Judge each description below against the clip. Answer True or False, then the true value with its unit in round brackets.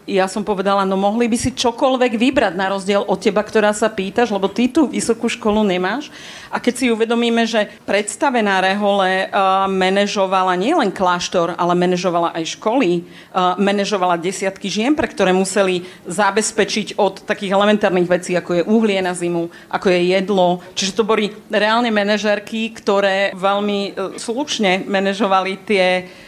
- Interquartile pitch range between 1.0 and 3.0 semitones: True (2.6 semitones)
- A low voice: False (200 Hz)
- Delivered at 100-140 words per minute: False (155 wpm)